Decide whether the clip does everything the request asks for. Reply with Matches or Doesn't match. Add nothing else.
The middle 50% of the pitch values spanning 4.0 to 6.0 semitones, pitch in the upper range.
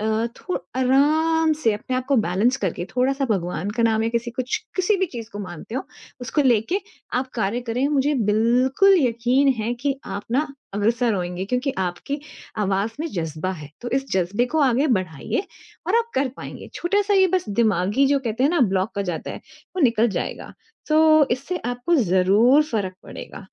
Matches